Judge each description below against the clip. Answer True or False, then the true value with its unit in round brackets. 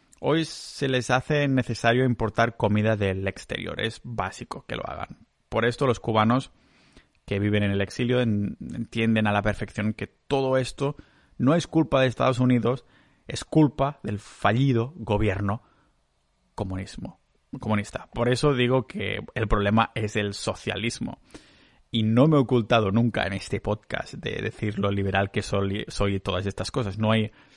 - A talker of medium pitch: False (110 Hz)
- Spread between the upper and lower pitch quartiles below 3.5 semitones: False (3.9 semitones)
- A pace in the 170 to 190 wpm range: False (160 wpm)